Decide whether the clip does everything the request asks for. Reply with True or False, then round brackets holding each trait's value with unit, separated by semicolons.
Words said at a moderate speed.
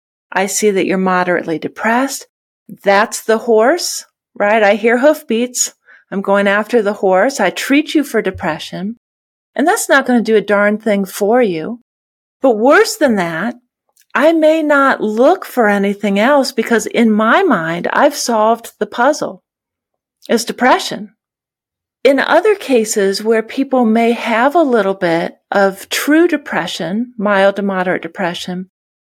True (150 wpm)